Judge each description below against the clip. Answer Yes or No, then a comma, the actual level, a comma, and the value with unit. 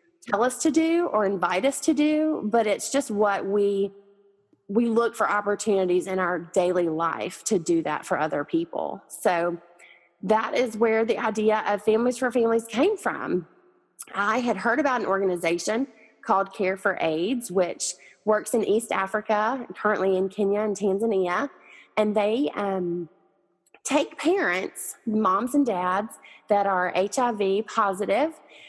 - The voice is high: Yes, high, 210 Hz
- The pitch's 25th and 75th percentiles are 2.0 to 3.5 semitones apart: No, average, 4.0 semitones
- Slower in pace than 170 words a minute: Yes, average, 150 wpm